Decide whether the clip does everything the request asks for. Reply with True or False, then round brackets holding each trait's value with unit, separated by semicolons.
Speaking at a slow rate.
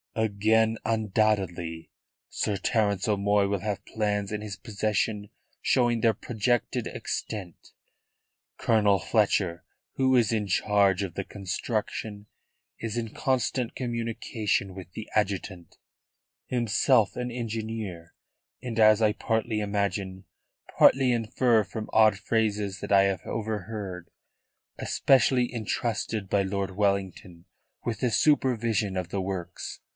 True (120 wpm)